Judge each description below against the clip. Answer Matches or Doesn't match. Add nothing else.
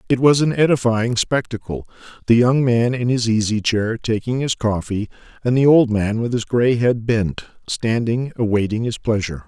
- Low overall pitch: Matches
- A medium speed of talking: Matches